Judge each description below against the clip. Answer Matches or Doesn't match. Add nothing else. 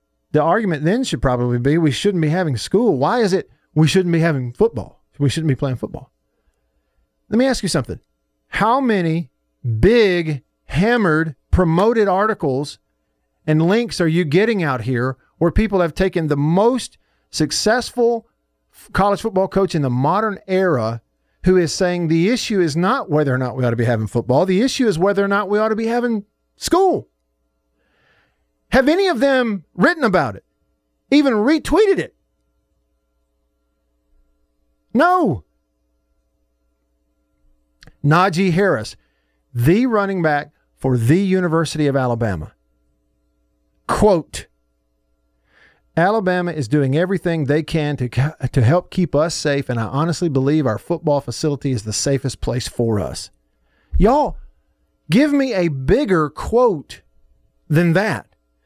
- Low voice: Doesn't match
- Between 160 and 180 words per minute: Doesn't match